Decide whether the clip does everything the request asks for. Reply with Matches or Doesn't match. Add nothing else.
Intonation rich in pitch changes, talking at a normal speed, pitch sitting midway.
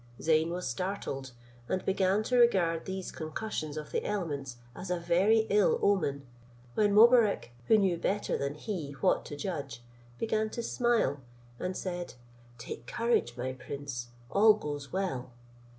Matches